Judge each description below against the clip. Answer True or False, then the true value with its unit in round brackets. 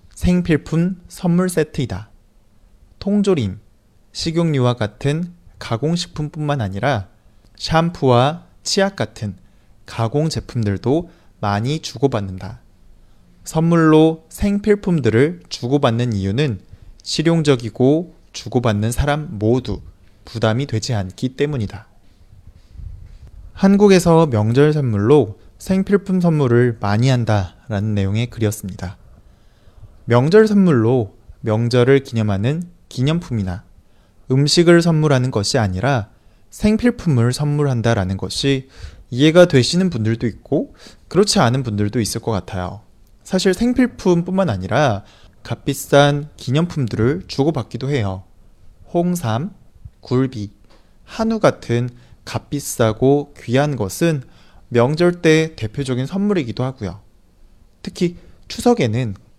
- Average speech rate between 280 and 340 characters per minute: False (245 characters per minute)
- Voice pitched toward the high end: False (120 Hz)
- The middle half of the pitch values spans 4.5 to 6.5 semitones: False (7.2 semitones)